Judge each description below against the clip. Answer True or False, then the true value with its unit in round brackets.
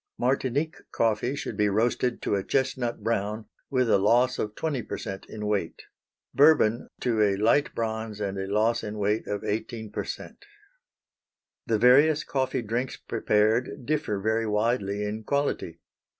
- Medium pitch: False (110 Hz)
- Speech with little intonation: False (3.3 semitones)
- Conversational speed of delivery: True (150 wpm)